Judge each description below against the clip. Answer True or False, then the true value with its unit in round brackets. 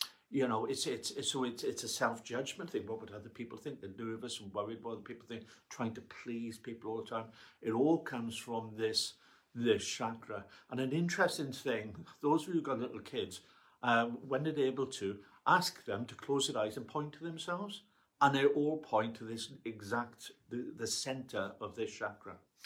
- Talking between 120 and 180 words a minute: False (205 wpm)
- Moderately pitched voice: False (120 Hz)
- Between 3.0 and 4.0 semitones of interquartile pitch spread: True (3.7 semitones)